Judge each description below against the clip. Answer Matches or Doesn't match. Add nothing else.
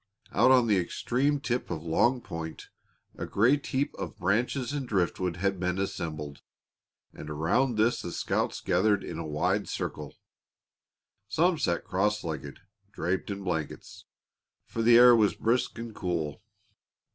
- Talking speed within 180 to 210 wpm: Doesn't match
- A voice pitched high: Doesn't match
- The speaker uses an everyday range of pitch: Doesn't match